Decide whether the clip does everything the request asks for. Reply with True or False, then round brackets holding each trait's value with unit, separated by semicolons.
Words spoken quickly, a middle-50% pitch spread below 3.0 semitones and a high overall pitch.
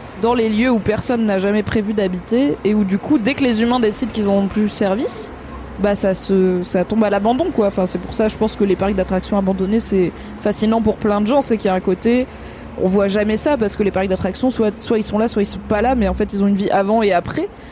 True (290 wpm; 2.5 semitones; 210 Hz)